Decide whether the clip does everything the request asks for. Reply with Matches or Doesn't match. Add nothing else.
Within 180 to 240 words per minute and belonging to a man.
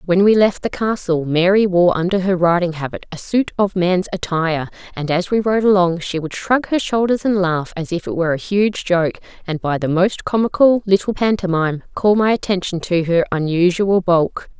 Doesn't match